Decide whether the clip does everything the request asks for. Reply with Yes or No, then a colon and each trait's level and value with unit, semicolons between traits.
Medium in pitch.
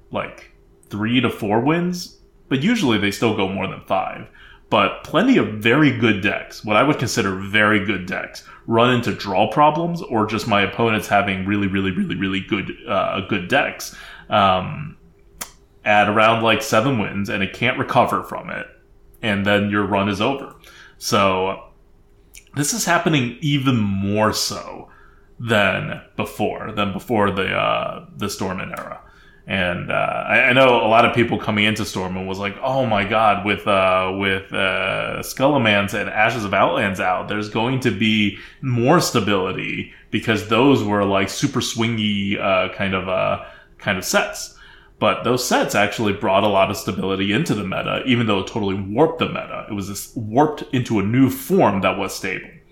No: low, 105 Hz